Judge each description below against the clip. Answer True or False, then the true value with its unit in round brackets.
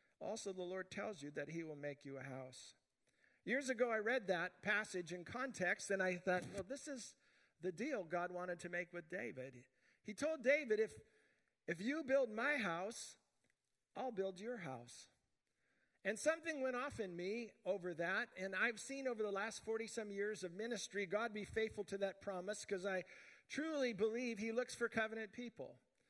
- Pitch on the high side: True (210 Hz)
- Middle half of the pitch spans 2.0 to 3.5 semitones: False (5.2 semitones)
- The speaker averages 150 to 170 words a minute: False (185 wpm)